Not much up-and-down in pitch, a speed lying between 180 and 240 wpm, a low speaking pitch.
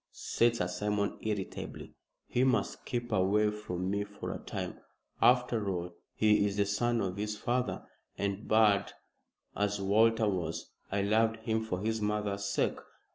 No: narrow, 1.9 semitones; average, 155 wpm; low, 105 Hz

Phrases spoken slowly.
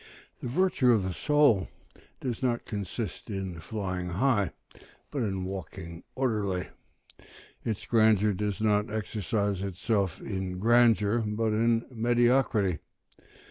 Yes: slow, 120 wpm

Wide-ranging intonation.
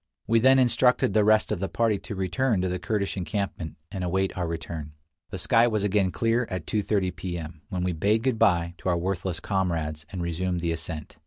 No: average, 3.8 semitones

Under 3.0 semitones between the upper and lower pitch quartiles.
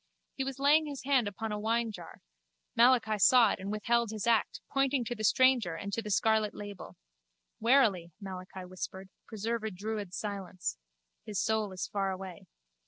No: average, 3.4 semitones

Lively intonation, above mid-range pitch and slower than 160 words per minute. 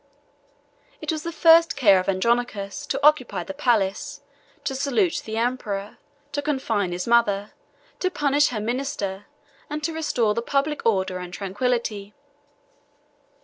Yes: wide, 6.2 semitones; high, 240 Hz; average, 140 wpm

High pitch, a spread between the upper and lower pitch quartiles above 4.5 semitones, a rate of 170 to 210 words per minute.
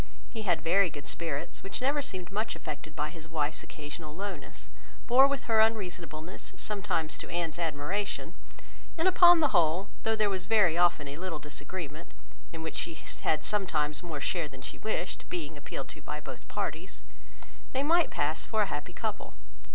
No: medium, 170 Hz; wide, 5.4 semitones; average, 175 wpm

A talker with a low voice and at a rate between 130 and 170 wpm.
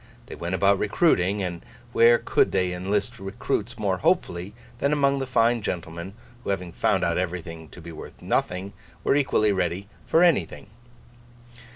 Yes: very low, 95 Hz; average, 160 wpm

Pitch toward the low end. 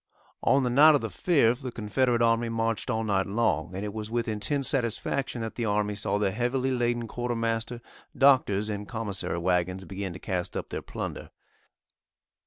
Yes: low, 115 Hz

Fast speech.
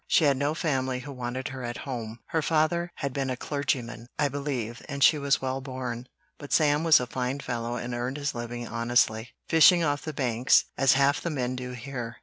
Yes: fast, 210 wpm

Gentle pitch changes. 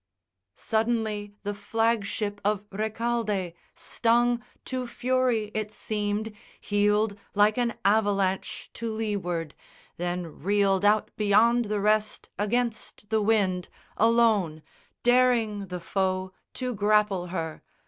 Yes: narrow, 2.2 semitones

